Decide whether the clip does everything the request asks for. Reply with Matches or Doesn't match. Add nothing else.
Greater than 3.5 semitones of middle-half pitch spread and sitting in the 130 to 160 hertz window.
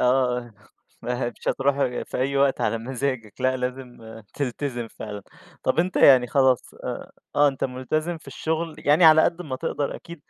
Doesn't match